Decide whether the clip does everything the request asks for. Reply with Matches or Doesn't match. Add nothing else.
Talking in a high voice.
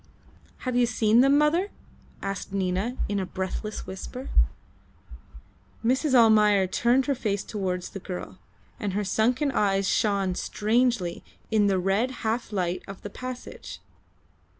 Matches